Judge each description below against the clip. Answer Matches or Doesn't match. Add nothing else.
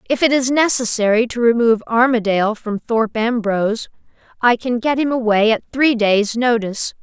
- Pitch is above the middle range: Matches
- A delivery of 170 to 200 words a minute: Doesn't match